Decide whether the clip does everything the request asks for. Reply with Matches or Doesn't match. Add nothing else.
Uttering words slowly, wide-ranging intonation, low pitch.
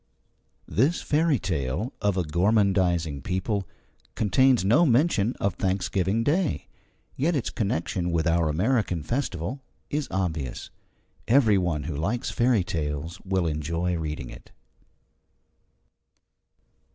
Matches